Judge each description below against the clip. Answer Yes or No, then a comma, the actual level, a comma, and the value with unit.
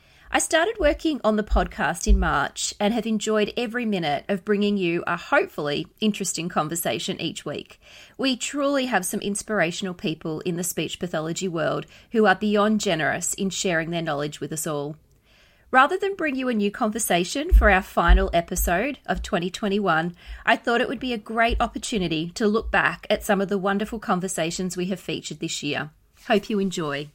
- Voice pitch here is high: Yes, high, 200 Hz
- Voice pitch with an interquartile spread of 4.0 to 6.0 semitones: Yes, average, 4.6 semitones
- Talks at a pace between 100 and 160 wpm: No, average, 180 wpm